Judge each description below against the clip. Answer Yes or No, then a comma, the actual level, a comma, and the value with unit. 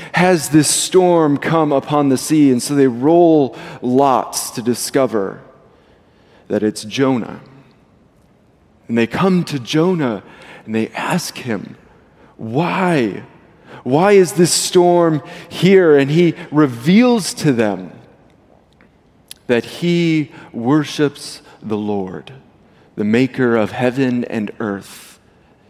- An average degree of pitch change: No, wide, 5.7 semitones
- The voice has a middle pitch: Yes, medium, 145 Hz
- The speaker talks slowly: Yes, slow, 110 wpm